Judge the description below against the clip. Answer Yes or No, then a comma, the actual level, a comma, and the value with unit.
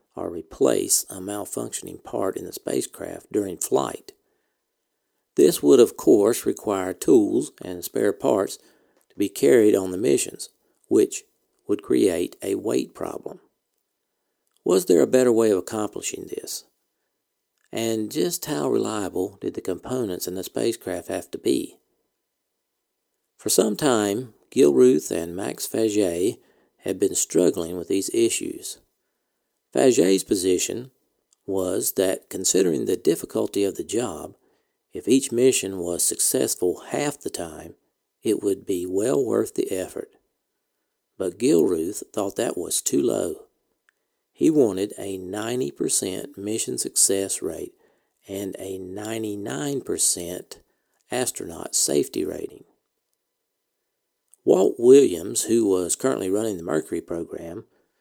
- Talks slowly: Yes, slow, 125 wpm